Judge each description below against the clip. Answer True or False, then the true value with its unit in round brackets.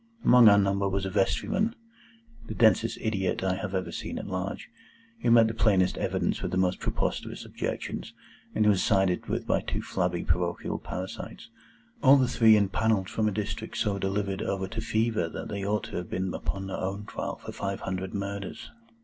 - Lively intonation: False (2.9 semitones)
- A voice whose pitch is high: False (100 Hz)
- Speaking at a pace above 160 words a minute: True (185 wpm)